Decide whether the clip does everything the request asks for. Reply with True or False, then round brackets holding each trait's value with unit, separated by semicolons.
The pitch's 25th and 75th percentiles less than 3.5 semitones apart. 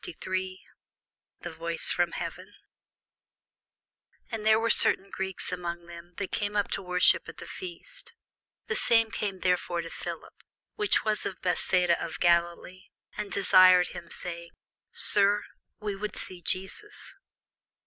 True (3.1 semitones)